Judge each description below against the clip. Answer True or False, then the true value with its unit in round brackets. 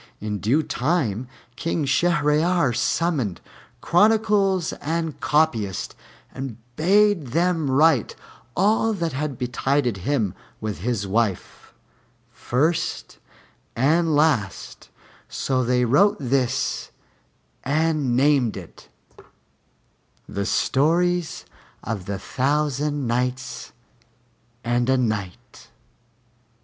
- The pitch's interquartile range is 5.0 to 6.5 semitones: True (5.3 semitones)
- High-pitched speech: False (140 Hz)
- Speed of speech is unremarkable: False (90 wpm)